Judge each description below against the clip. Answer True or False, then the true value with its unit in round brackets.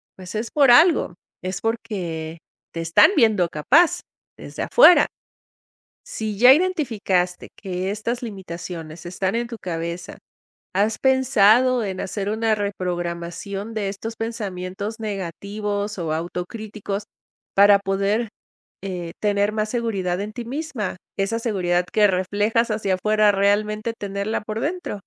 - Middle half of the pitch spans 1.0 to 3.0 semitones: False (3.5 semitones)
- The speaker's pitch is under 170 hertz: False (205 Hz)